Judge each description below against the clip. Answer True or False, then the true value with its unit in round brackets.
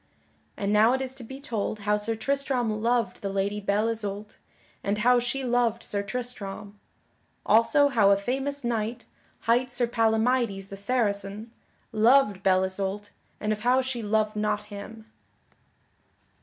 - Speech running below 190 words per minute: True (150 wpm)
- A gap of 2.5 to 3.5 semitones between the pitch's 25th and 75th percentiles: True (3.1 semitones)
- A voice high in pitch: True (220 Hz)